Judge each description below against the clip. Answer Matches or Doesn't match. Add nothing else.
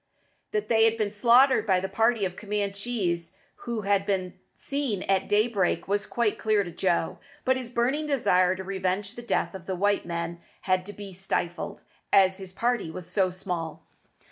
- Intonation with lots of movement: Doesn't match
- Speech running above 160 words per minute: Matches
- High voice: Matches